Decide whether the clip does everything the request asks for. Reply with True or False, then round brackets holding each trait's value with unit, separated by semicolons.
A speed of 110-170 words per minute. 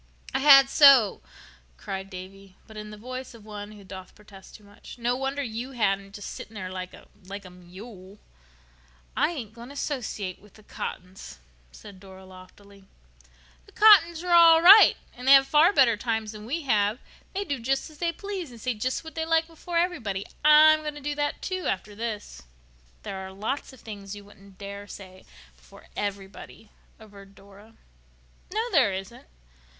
False (185 wpm)